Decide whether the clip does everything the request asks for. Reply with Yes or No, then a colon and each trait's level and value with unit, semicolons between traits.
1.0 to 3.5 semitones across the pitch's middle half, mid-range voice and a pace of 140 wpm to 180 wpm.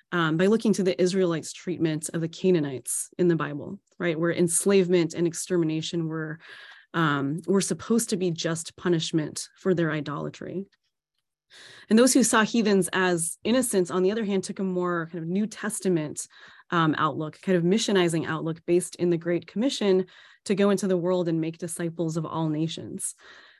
Yes: narrow, 2.6 semitones; medium, 175 Hz; average, 175 wpm